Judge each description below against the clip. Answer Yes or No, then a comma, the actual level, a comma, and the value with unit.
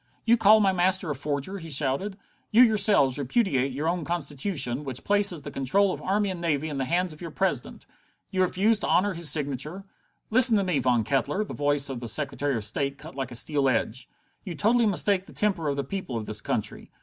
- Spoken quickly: Yes, fast, 220 wpm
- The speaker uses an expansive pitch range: Yes, wide, 6.0 semitones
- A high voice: No, medium, 155 Hz